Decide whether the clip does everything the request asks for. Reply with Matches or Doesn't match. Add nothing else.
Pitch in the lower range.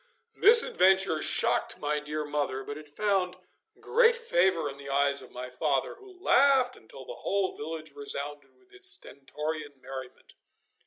Doesn't match